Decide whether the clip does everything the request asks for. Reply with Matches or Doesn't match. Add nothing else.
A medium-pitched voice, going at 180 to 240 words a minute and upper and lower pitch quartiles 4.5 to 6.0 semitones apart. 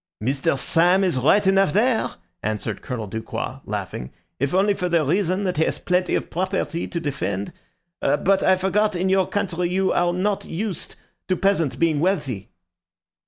Doesn't match